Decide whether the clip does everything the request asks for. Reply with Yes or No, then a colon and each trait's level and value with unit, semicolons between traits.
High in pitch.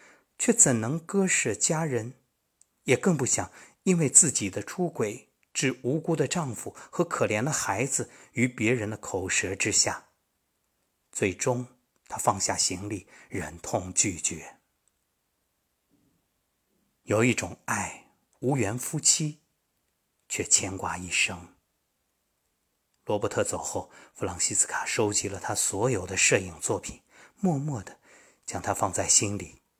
No: low, 120 Hz